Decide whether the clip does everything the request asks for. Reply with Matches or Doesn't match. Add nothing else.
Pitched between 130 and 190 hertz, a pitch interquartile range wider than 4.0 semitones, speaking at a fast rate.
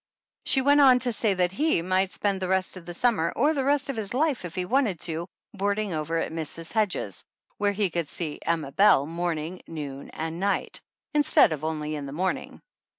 Matches